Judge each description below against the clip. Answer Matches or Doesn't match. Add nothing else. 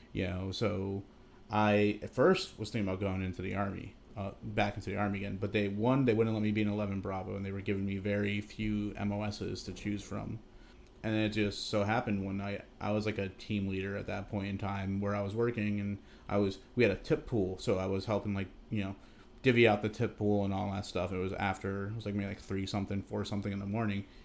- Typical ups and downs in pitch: Doesn't match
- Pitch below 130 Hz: Matches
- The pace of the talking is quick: Matches